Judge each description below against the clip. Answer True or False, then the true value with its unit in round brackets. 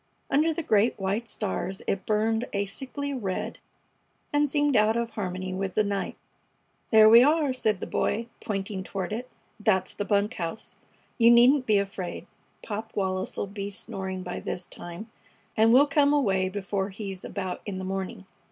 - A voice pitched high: True (205 Hz)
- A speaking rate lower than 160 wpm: False (170 wpm)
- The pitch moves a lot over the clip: False (3.5 semitones)